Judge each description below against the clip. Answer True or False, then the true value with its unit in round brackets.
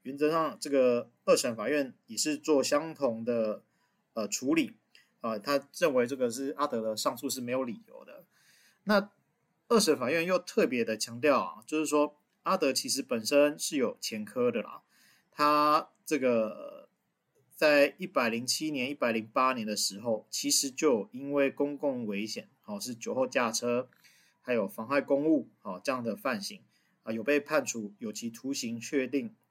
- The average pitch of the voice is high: False (145 Hz)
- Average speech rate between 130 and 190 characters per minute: False (245 characters per minute)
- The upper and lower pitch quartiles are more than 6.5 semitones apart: True (8.8 semitones)